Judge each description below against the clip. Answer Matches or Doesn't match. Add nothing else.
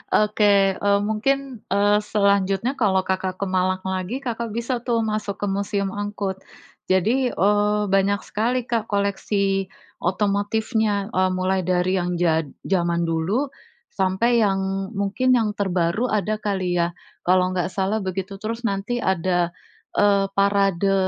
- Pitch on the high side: Matches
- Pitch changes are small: Matches